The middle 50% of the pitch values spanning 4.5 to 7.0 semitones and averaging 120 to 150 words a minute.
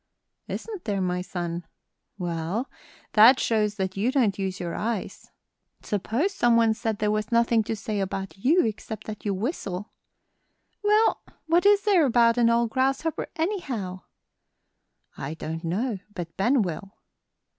Yes: average, 5.1 semitones; average, 145 wpm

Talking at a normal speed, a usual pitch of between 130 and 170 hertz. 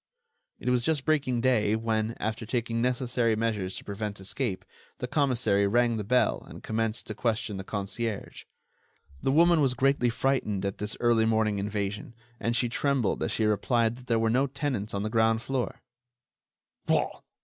No: average, 170 wpm; low, 115 Hz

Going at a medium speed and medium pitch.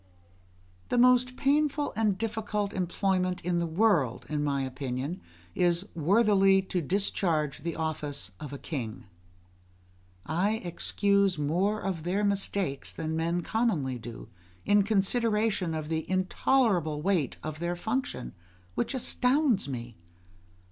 No: slow, 125 wpm; medium, 180 Hz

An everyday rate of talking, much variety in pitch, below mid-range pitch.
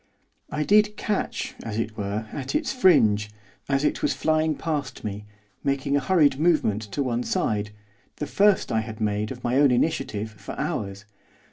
Yes: average, 170 wpm; wide, 6.5 semitones; low, 130 Hz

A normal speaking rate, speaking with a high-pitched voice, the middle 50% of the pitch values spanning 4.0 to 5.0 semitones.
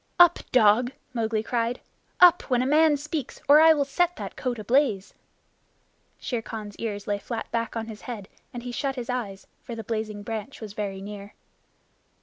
Yes: average, 180 wpm; high, 230 Hz; average, 4.3 semitones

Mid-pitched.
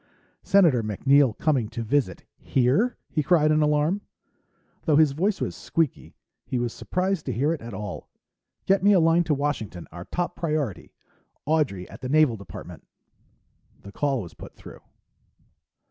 Yes: medium, 145 Hz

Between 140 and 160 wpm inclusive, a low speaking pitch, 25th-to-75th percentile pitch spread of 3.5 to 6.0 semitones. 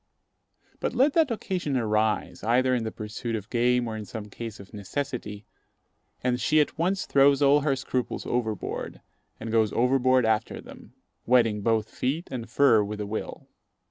No: average, 170 wpm; low, 120 Hz; average, 3.8 semitones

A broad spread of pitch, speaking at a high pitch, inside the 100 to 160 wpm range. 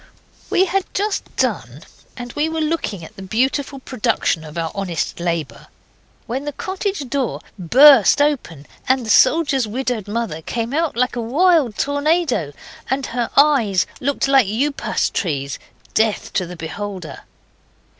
Yes: wide, 6.9 semitones; high, 245 Hz; average, 145 wpm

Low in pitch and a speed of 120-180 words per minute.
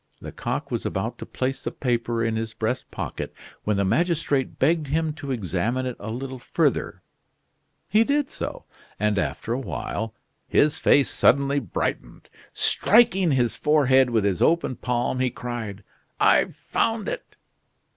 Yes: low, 130 Hz; average, 150 wpm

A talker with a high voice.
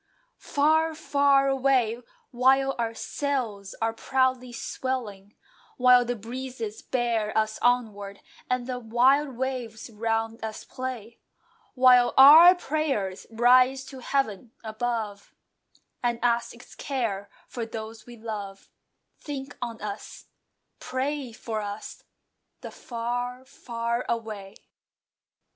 Yes: high, 240 Hz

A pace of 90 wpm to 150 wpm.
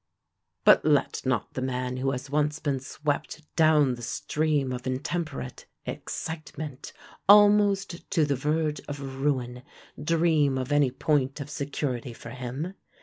Yes: average, 140 wpm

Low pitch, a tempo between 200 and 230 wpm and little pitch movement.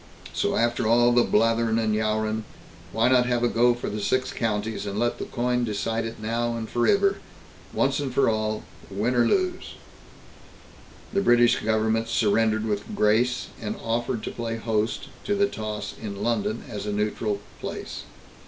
No: low, 115 Hz; average, 170 wpm; narrow, 1.9 semitones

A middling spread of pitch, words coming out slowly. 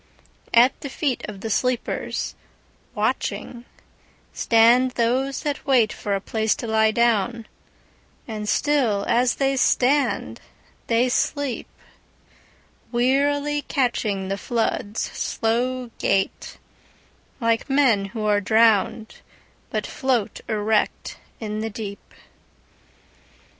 Yes: average, 3.0 semitones; slow, 90 wpm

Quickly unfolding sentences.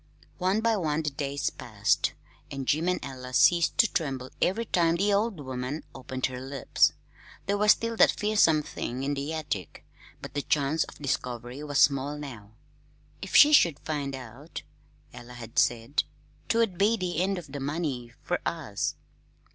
No: average, 170 wpm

